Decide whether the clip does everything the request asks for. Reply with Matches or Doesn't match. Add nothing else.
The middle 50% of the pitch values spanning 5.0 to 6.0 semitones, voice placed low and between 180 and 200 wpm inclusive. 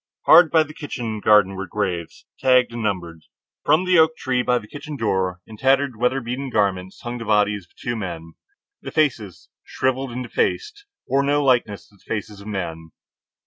Matches